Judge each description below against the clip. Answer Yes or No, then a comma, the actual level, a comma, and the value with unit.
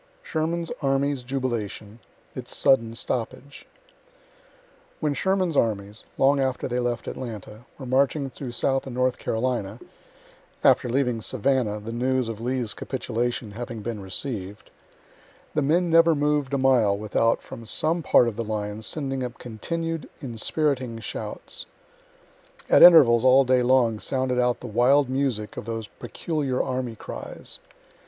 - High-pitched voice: No, low, 125 Hz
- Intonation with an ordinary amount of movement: Yes, average, 3.2 semitones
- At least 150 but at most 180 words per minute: No, slow, 135 wpm